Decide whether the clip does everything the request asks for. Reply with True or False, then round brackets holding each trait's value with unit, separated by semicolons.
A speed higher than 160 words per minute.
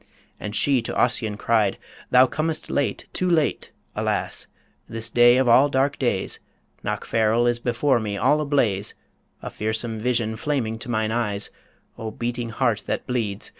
False (155 wpm)